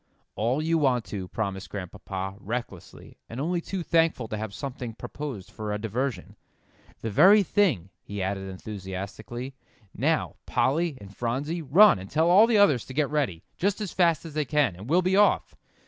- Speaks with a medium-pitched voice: No, low, 130 Hz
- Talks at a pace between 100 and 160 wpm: No, average, 180 wpm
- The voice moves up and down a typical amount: No, wide, 8.2 semitones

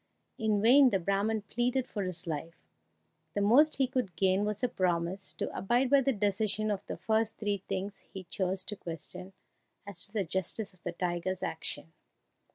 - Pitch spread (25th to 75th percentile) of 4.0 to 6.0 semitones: No, average, 3.1 semitones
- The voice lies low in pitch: No, high, 200 Hz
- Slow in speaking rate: No, average, 180 wpm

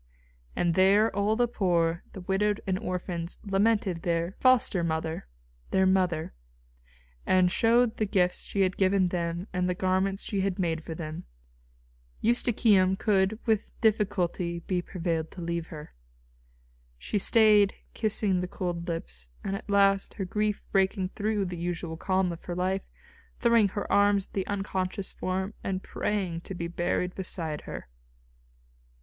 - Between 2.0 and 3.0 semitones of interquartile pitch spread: Yes, narrow, 2.6 semitones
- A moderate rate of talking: Yes, average, 150 wpm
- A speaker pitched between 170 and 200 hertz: Yes, high, 190 Hz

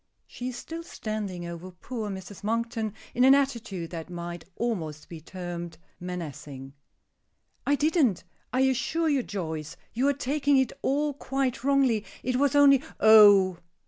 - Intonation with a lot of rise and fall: Yes, wide, 7.2 semitones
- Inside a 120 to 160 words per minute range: Yes, average, 150 wpm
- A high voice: Yes, high, 220 Hz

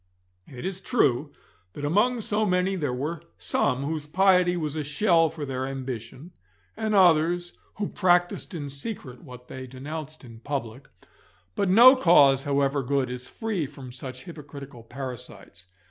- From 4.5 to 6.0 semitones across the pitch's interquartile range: Yes, average, 5.3 semitones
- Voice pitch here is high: No, medium, 145 Hz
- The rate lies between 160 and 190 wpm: No, average, 150 wpm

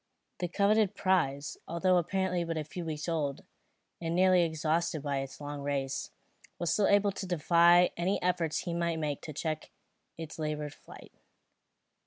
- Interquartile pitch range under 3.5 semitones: Yes, average, 2.9 semitones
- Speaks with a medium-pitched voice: Yes, medium, 170 Hz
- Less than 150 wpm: No, average, 160 wpm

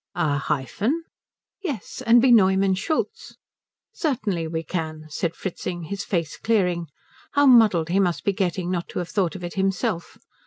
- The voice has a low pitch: No, medium, 185 Hz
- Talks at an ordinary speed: Yes, average, 160 wpm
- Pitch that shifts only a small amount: No, average, 4.0 semitones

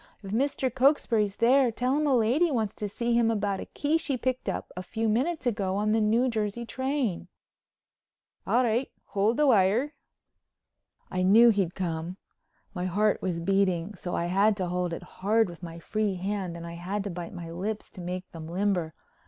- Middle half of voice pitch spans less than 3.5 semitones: No, average, 4.6 semitones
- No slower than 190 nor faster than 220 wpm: Yes, average, 195 wpm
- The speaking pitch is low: No, high, 205 Hz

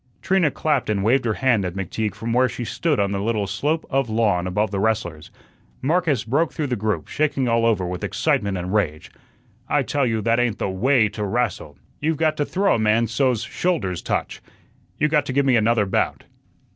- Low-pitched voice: Yes, low, 115 Hz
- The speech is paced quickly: Yes, fast, 210 wpm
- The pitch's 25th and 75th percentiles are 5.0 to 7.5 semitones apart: Yes, average, 5.3 semitones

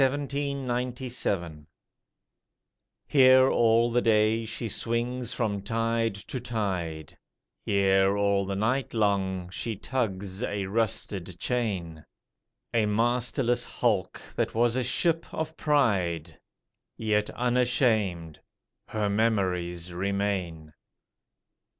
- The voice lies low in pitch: Yes, low, 110 Hz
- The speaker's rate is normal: No, slow, 100 wpm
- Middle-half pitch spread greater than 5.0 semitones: No, average, 4.1 semitones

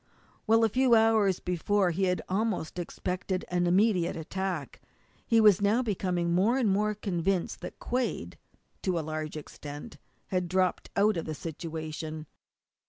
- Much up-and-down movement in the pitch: No, average, 4.0 semitones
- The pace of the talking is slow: No, average, 150 wpm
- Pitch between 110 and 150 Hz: No, medium, 185 Hz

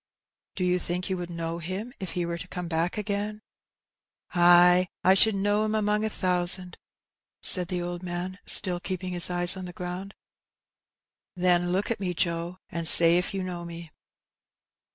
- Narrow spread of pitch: Yes, narrow, 1.5 semitones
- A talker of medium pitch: Yes, medium, 180 Hz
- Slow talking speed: No, average, 190 wpm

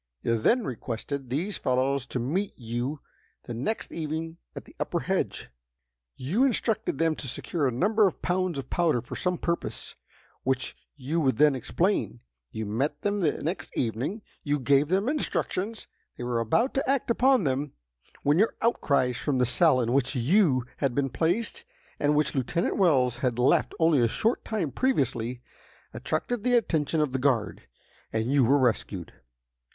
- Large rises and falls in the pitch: Yes, wide, 6.3 semitones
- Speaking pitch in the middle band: Yes, medium, 145 Hz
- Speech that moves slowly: No, average, 170 wpm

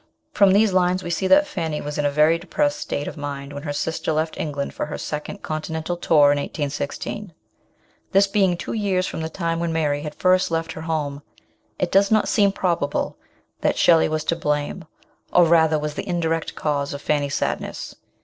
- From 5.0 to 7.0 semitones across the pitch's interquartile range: No, average, 3.4 semitones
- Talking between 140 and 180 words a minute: No, average, 195 wpm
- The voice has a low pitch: No, medium, 160 Hz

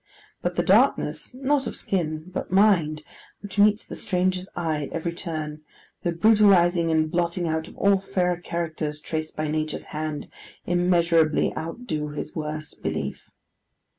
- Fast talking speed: No, slow, 135 wpm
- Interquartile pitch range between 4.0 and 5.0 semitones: No, average, 3.0 semitones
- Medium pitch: Yes, medium, 170 Hz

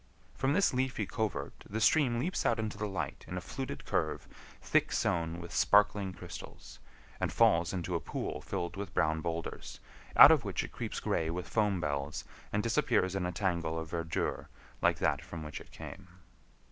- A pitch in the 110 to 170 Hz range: No, very low, 90 Hz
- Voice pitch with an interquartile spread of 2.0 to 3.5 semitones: No, average, 4.3 semitones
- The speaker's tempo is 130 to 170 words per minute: No, average, 185 wpm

